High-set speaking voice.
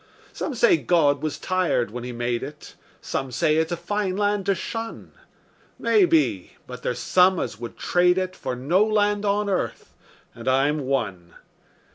No: medium, 175 Hz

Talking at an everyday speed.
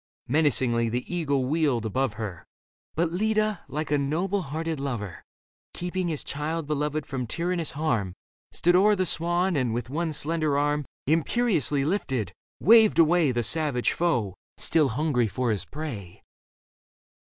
Yes: average, 145 wpm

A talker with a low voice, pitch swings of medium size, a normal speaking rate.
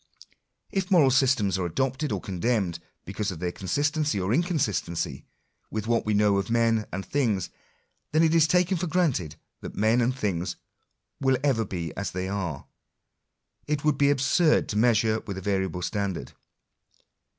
No: low, 110 Hz; wide, 7.0 semitones; average, 170 wpm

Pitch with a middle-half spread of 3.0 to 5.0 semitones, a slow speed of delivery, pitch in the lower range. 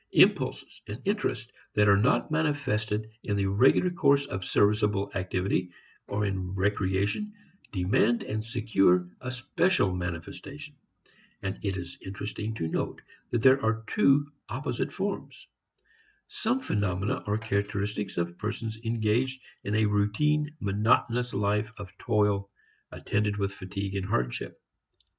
Yes: average, 3.5 semitones; slow, 130 wpm; low, 105 Hz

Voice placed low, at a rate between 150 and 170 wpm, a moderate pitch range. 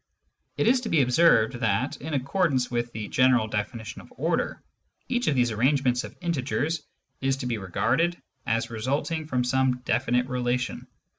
Yes: low, 130 Hz; average, 160 wpm; average, 3.7 semitones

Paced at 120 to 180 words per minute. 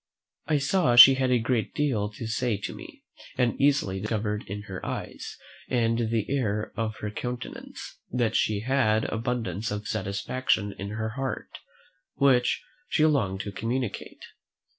Yes: average, 150 wpm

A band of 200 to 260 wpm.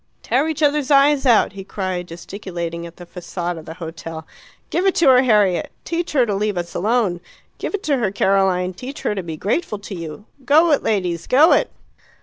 Yes: fast, 205 wpm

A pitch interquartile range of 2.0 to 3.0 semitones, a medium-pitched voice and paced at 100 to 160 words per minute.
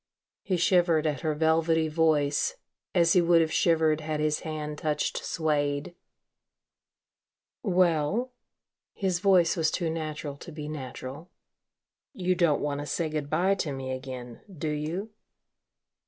Yes: narrow, 2.5 semitones; medium, 155 Hz; average, 140 wpm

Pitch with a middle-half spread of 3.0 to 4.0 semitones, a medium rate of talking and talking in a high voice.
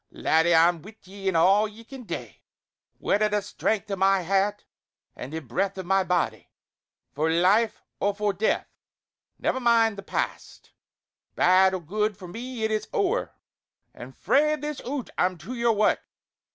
Yes: average, 3.4 semitones; average, 170 wpm; high, 200 Hz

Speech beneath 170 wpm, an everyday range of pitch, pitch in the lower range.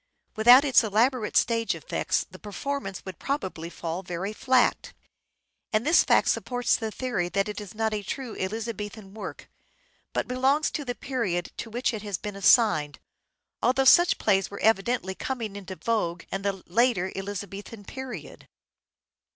No: average, 155 wpm; average, 4.2 semitones; high, 215 Hz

